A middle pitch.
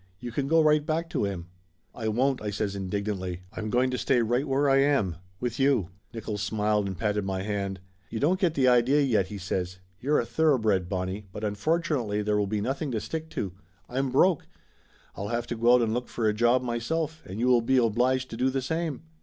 No: low, 120 Hz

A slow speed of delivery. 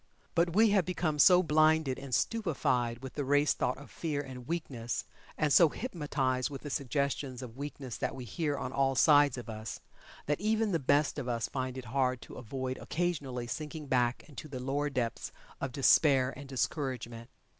No: average, 185 wpm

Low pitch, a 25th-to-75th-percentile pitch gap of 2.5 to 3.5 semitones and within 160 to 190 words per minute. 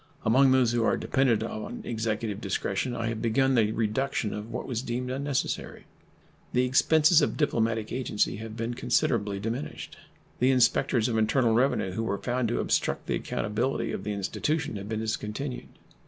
Yes: low, 115 Hz; average, 3.0 semitones; average, 170 wpm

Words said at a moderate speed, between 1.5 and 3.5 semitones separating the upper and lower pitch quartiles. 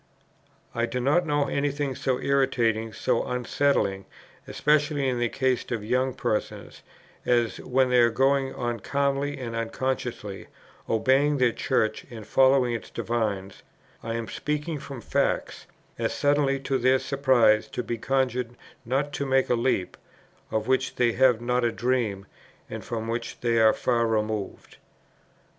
Yes: average, 150 wpm; average, 2.9 semitones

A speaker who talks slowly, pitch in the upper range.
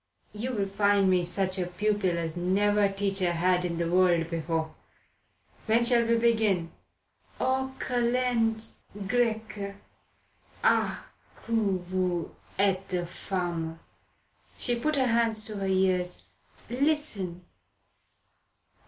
Yes: slow, 110 wpm; high, 195 Hz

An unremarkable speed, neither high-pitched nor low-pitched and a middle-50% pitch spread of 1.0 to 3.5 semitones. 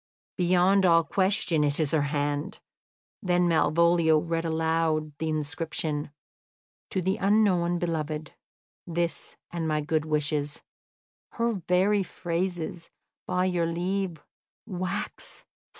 No: slow, 110 wpm; medium, 170 Hz; narrow, 2.6 semitones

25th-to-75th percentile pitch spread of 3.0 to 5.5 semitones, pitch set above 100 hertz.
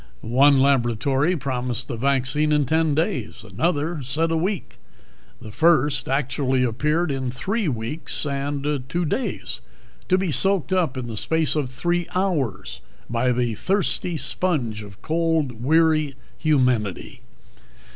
Yes: average, 4.5 semitones; medium, 140 Hz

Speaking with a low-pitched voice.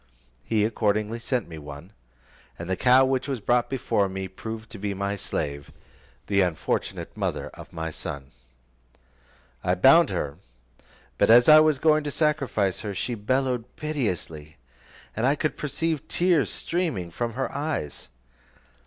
Yes: low, 110 Hz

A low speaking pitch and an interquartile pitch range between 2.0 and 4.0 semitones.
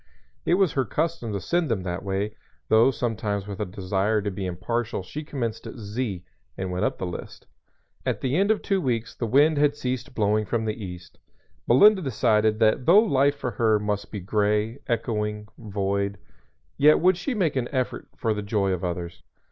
No: low, 110 Hz; average, 4.9 semitones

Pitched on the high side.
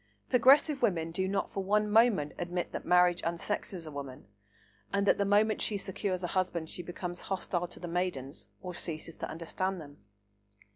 No: medium, 180 Hz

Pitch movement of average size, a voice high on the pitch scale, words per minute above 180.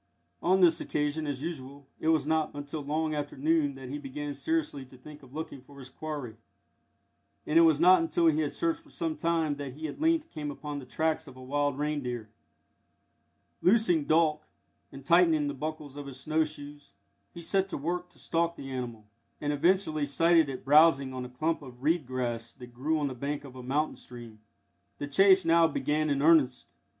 No: average, 3.0 semitones; medium, 150 Hz; average, 200 wpm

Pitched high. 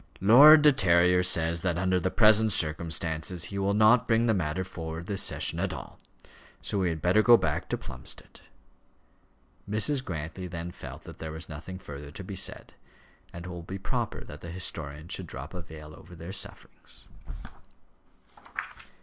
No: very low, 90 Hz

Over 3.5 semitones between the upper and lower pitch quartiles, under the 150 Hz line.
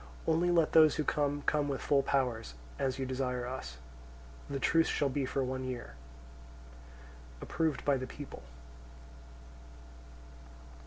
No: narrow, 2.5 semitones; low, 135 Hz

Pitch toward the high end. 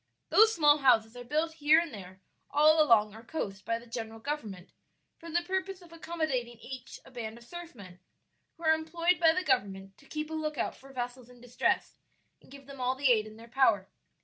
Yes: very high, 260 Hz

